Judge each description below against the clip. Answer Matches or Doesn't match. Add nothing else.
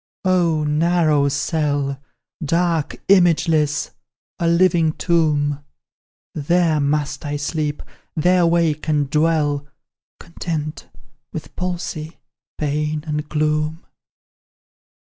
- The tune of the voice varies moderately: Doesn't match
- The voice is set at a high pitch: Doesn't match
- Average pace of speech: Doesn't match